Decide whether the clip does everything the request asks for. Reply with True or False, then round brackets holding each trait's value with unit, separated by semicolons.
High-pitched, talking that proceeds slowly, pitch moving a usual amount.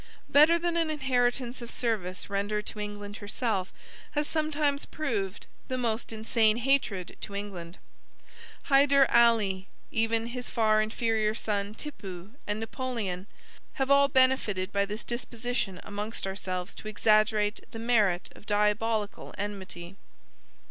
True (220 Hz; 125 wpm; 3.4 semitones)